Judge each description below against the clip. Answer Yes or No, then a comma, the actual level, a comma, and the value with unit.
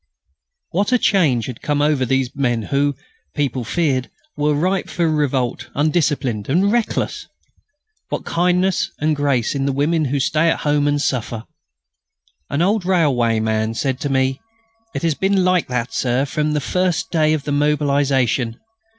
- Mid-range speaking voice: Yes, medium, 145 Hz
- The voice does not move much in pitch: No, average, 3.8 semitones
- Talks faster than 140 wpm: Yes, average, 160 wpm